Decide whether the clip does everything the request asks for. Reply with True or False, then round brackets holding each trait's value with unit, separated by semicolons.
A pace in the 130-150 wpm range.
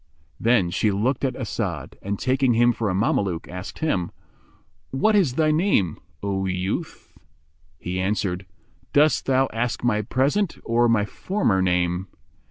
True (145 wpm)